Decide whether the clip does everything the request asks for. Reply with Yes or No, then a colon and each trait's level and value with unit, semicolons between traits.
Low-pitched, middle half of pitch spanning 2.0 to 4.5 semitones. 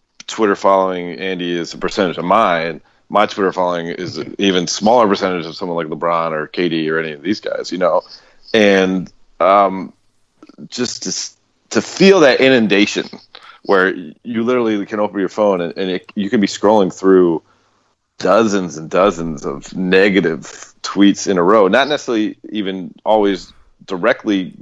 Yes: very low, 95 Hz; average, 3.1 semitones